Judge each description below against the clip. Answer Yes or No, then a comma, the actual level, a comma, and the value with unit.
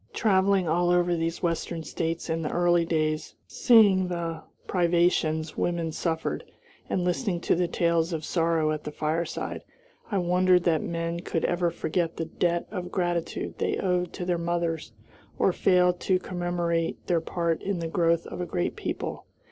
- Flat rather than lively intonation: Yes, narrow, 1.4 semitones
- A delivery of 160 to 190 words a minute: Yes, average, 165 wpm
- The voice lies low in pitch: No, medium, 170 Hz